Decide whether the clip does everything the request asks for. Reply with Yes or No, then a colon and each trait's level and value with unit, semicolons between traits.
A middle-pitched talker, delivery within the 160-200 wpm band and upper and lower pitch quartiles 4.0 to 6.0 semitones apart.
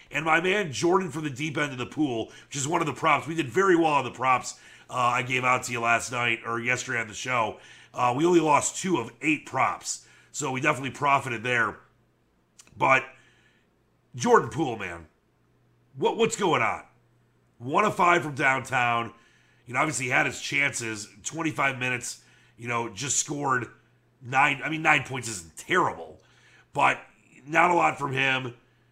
No: low, 130 Hz; average, 185 wpm; average, 4.5 semitones